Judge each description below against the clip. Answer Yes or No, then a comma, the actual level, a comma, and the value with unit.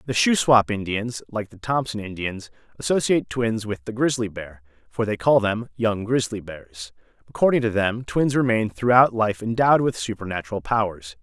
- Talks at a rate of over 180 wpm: No, average, 165 wpm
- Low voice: Yes, low, 110 Hz